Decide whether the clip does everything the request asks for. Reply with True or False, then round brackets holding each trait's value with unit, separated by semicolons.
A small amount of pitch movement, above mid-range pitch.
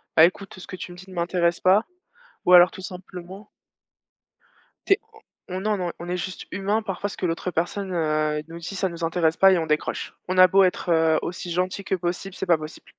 False (2.1 semitones; 180 Hz)